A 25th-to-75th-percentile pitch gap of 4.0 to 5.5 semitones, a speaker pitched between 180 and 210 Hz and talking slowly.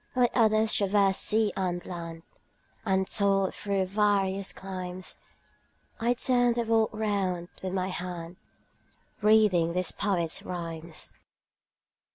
No: average, 2.9 semitones; high, 190 Hz; slow, 120 wpm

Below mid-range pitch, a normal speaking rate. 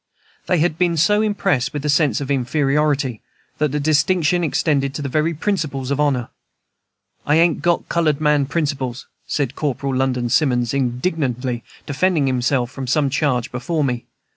No: medium, 145 Hz; average, 160 wpm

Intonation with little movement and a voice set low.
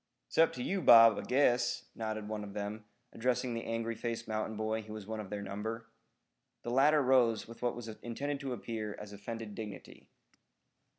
Yes: narrow, 2.1 semitones; low, 115 Hz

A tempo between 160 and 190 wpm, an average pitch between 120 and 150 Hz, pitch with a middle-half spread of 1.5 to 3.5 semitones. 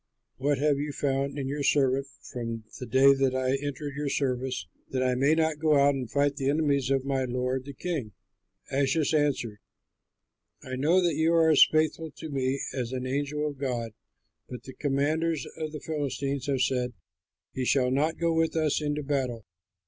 Yes: average, 185 wpm; medium, 140 Hz; narrow, 2.4 semitones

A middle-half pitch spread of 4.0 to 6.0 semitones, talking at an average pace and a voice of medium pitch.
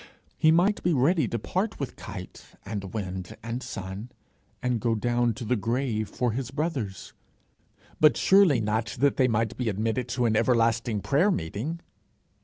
No: average, 4.3 semitones; average, 165 wpm; low, 120 Hz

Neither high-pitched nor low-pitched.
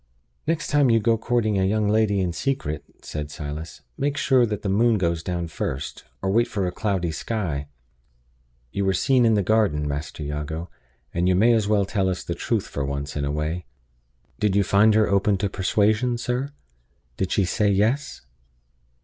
No: low, 100 Hz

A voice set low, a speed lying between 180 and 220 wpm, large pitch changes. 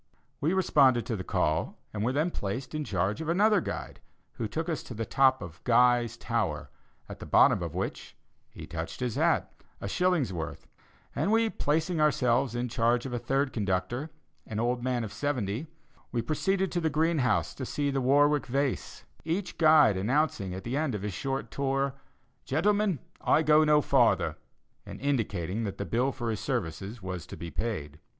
Yes: low, 130 Hz; average, 185 wpm; wide, 5.9 semitones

